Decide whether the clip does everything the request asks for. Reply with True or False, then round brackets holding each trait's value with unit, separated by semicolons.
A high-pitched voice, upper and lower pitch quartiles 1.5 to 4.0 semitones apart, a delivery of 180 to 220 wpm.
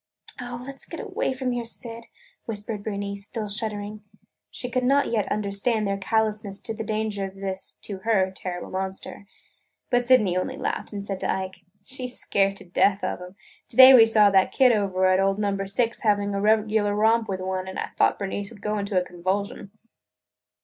True (205 Hz; 2.5 semitones; 200 wpm)